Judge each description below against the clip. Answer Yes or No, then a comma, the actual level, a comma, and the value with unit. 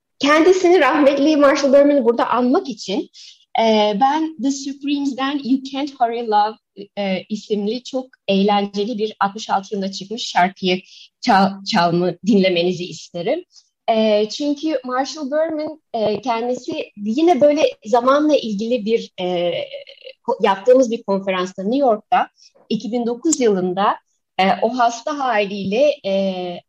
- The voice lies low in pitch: No, high, 235 Hz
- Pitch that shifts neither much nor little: No, wide, 5.7 semitones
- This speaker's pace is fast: No, average, 115 wpm